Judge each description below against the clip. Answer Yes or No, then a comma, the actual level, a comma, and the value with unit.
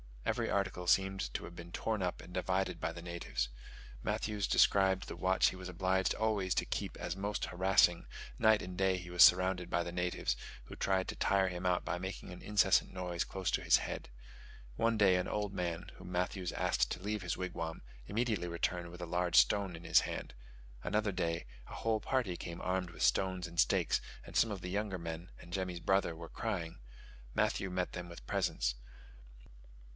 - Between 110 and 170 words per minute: No, average, 195 wpm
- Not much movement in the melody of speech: Yes, narrow, 1.8 semitones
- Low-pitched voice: Yes, very low, 90 Hz